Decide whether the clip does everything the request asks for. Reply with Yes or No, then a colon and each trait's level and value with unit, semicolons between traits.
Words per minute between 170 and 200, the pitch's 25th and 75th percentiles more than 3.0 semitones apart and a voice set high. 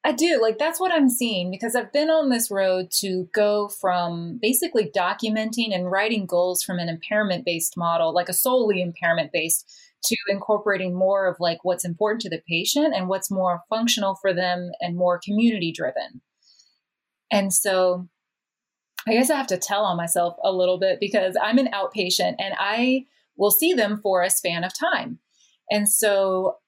Yes: average, 175 wpm; average, 4.2 semitones; high, 195 Hz